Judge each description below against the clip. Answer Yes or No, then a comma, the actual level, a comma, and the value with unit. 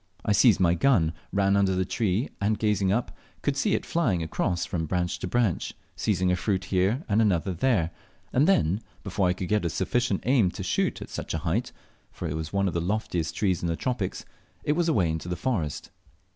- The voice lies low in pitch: Yes, very low, 95 Hz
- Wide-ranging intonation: No, average, 4.0 semitones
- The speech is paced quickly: Yes, fast, 215 wpm